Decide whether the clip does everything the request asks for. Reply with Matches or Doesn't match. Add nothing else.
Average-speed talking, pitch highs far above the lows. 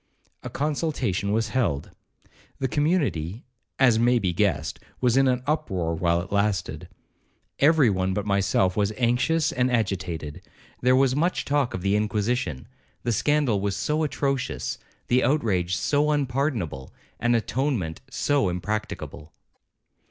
Doesn't match